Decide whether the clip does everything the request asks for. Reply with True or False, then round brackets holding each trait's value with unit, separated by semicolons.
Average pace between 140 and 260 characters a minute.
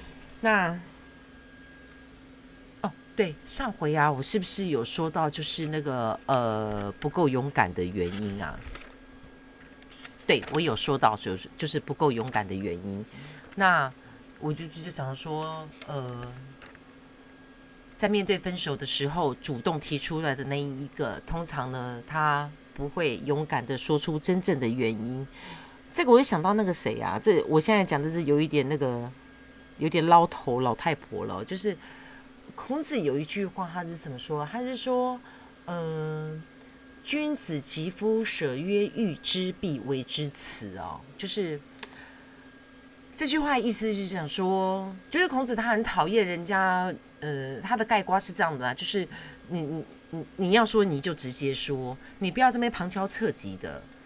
True (220 characters per minute)